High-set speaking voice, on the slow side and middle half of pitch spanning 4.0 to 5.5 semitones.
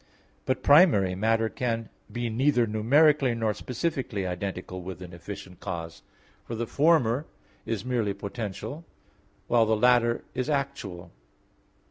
No: low, 115 Hz; slow, 125 wpm; average, 4.5 semitones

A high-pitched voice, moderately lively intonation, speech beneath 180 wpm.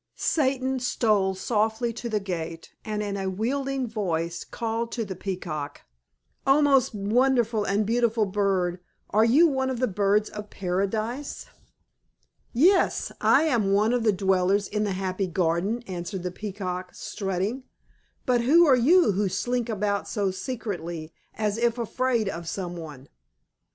Yes: high, 210 Hz; average, 4.2 semitones; average, 150 wpm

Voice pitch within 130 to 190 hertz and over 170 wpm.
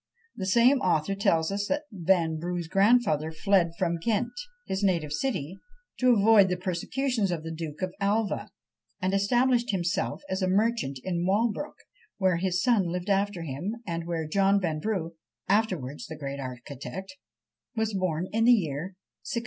No: medium, 185 Hz; average, 155 wpm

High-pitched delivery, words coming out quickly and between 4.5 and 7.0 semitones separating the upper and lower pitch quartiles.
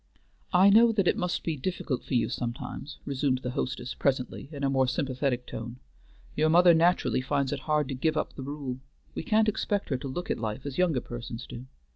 No: medium, 140 Hz; fast, 210 wpm; average, 4.8 semitones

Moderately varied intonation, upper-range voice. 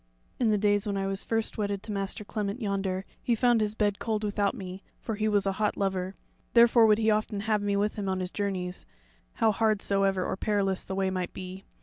No: narrow, 1.8 semitones; high, 205 Hz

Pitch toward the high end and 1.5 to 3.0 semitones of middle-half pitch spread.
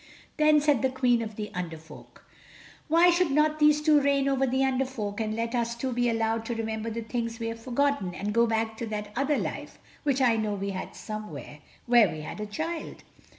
No: high, 235 Hz; average, 4.1 semitones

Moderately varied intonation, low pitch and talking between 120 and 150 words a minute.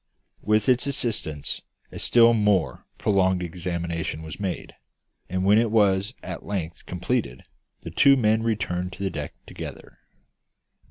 Yes: average, 3.9 semitones; low, 100 Hz; average, 140 wpm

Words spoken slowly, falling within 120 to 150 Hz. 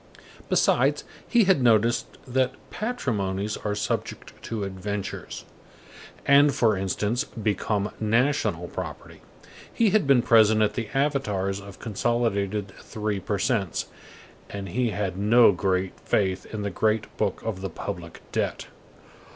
No: slow, 130 wpm; low, 105 Hz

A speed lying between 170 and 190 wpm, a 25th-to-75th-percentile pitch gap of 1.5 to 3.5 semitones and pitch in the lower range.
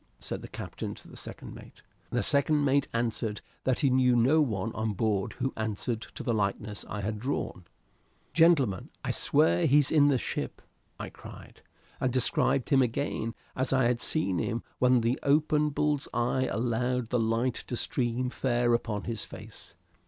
Yes: average, 175 wpm; average, 3.2 semitones; low, 120 Hz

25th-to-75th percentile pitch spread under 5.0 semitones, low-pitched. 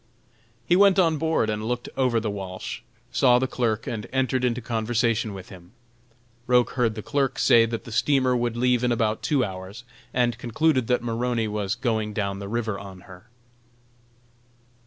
Yes: average, 2.8 semitones; low, 115 Hz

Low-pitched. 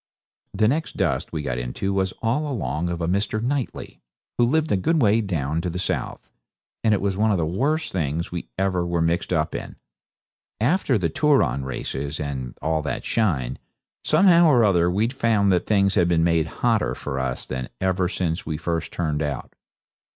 Yes: very low, 90 Hz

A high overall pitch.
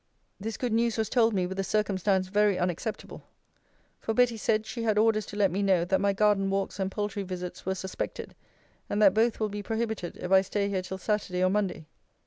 Yes: high, 200 Hz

